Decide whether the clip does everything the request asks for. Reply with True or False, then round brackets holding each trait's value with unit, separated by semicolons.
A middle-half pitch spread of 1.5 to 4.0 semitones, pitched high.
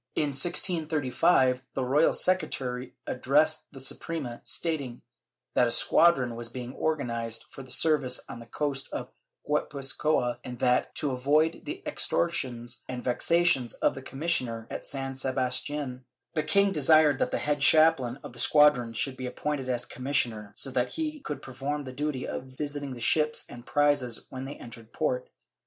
False (3.4 semitones; 135 Hz)